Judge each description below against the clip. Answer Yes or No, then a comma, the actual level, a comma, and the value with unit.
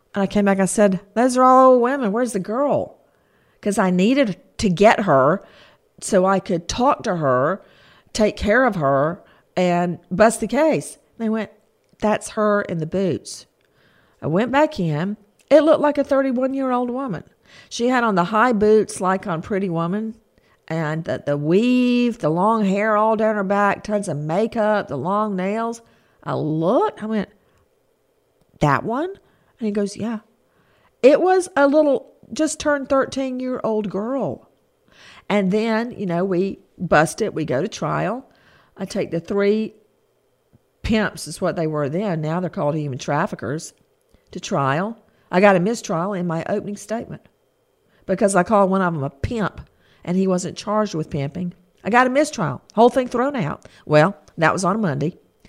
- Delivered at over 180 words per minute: No, average, 175 wpm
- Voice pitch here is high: Yes, high, 205 Hz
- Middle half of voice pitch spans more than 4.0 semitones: Yes, average, 4.5 semitones